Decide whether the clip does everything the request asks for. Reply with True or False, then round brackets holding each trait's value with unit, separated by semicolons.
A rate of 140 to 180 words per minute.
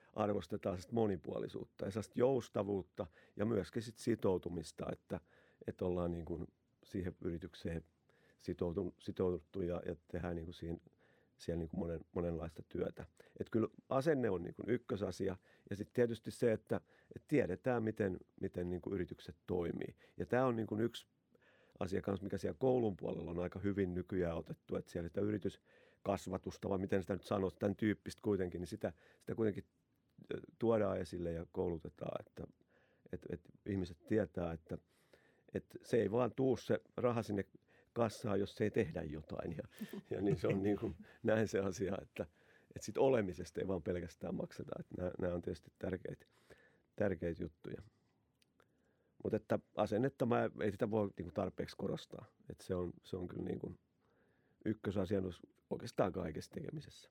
True (150 wpm)